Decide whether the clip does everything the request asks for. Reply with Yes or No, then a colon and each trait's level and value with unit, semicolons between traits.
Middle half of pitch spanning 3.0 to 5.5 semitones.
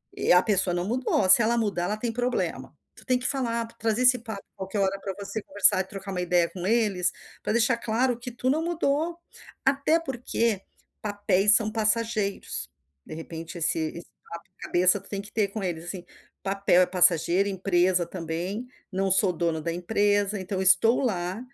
Yes: average, 4.3 semitones